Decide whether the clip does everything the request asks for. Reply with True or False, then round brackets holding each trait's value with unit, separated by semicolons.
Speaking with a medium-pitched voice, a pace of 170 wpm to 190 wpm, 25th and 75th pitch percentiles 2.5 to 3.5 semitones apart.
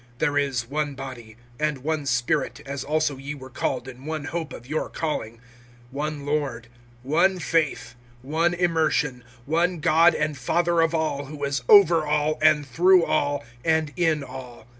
False (150 Hz; 160 wpm; 2.9 semitones)